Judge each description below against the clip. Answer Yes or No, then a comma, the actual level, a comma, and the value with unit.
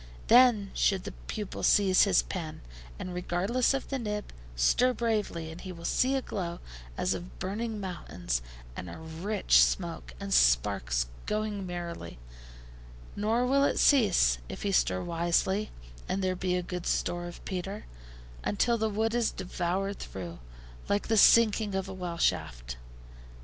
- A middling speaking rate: Yes, average, 155 wpm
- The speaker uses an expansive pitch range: No, average, 4.1 semitones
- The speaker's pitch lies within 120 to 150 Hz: No, medium, 185 Hz